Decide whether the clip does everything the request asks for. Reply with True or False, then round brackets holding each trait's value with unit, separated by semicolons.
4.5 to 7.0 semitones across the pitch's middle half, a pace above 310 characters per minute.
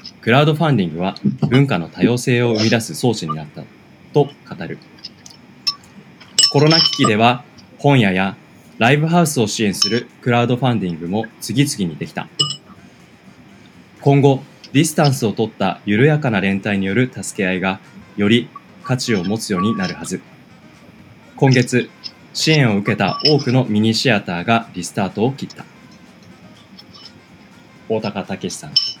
False (5.3 semitones; 295 characters per minute)